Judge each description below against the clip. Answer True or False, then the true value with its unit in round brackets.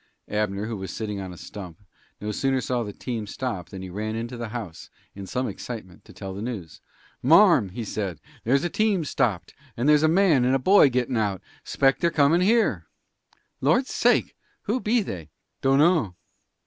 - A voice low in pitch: True (120 Hz)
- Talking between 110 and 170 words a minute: False (185 wpm)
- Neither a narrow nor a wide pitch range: False (6.6 semitones)